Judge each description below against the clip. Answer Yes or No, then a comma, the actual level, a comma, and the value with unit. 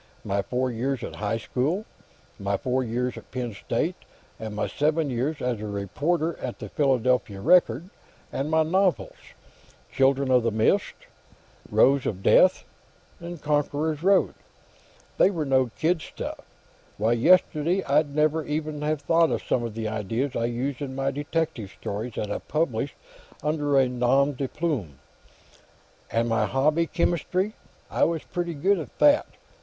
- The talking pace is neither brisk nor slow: Yes, average, 155 wpm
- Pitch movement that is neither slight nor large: Yes, average, 5.0 semitones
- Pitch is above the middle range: No, medium, 140 Hz